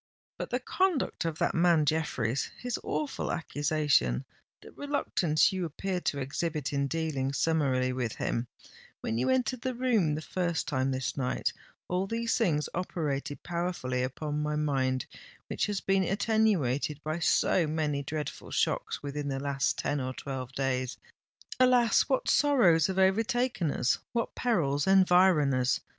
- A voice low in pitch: No, medium, 155 Hz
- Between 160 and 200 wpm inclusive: No, average, 140 wpm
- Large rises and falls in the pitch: Yes, wide, 5.8 semitones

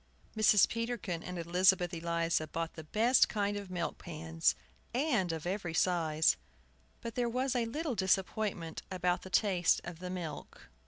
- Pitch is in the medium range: Yes, medium, 180 Hz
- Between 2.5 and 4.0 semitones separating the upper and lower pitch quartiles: No, average, 4.4 semitones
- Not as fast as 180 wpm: Yes, average, 150 wpm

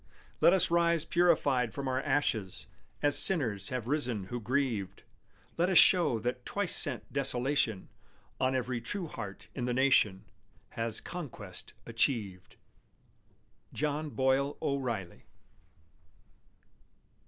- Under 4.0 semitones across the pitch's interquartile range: No, average, 4.3 semitones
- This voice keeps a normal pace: No, slow, 115 wpm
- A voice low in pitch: Yes, low, 130 Hz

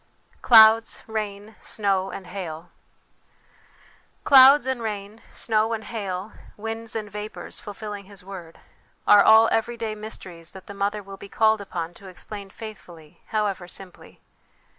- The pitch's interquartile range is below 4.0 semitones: Yes, narrow, 2.4 semitones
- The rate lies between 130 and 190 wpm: Yes, slow, 135 wpm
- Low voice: No, high, 205 Hz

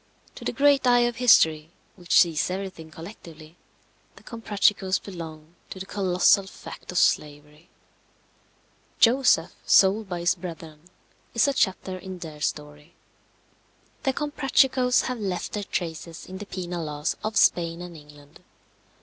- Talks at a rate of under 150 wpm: Yes, average, 140 wpm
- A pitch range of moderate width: Yes, average, 4.9 semitones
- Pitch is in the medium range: Yes, medium, 180 Hz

